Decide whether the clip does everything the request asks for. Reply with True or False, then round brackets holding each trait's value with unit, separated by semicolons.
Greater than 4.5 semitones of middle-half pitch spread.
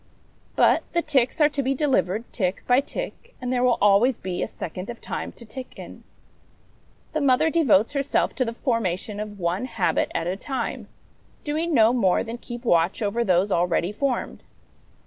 True (5.3 semitones)